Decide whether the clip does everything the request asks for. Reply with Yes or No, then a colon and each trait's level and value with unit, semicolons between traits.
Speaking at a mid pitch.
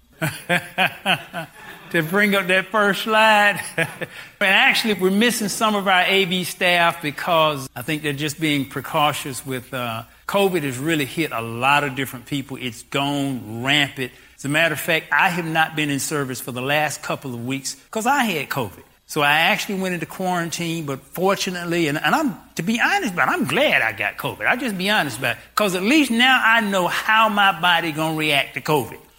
Yes: medium, 165 Hz